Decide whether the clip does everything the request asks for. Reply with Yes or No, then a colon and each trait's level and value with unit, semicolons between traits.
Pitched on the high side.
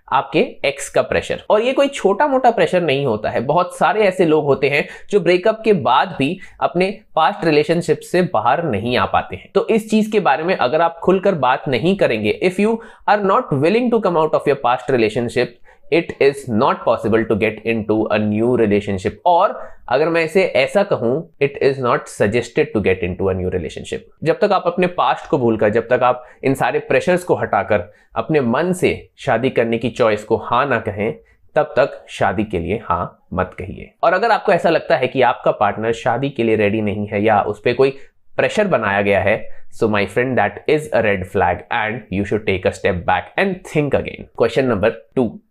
No: medium, 140 Hz